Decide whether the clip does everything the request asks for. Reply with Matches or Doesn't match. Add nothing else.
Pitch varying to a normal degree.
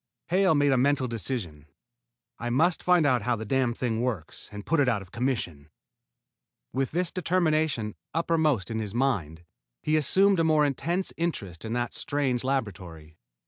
Doesn't match